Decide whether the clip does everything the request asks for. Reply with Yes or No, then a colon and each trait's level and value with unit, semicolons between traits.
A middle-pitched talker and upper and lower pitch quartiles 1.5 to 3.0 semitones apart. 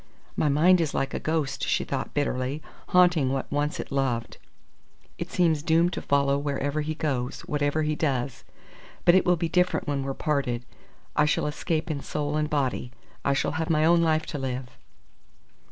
Yes: medium, 150 Hz; narrow, 2.6 semitones